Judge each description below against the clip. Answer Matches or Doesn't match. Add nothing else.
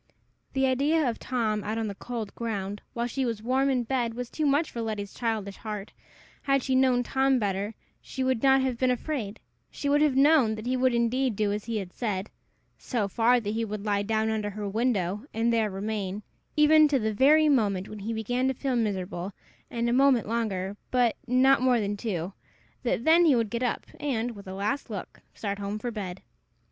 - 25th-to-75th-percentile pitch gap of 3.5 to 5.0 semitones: Matches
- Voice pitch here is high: Matches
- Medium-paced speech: Doesn't match